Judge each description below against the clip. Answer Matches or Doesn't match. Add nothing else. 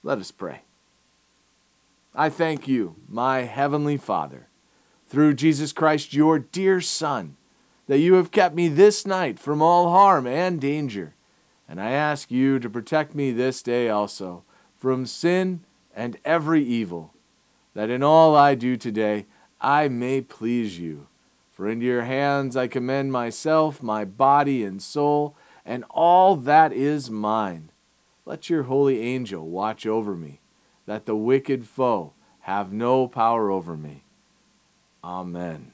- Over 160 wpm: Doesn't match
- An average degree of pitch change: Doesn't match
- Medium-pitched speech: Doesn't match